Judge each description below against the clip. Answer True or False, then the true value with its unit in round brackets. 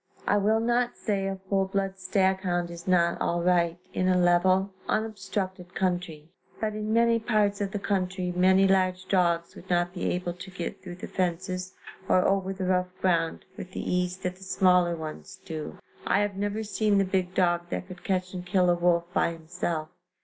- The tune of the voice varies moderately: False (1.6 semitones)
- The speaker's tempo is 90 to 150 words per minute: False (195 wpm)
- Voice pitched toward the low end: False (185 Hz)